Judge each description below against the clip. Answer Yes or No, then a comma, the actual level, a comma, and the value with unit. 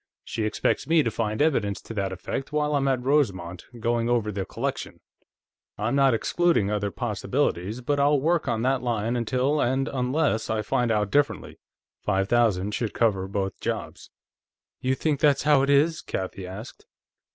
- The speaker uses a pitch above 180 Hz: No, low, 120 Hz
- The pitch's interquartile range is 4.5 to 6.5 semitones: Yes, average, 5.0 semitones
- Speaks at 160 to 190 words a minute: Yes, average, 170 wpm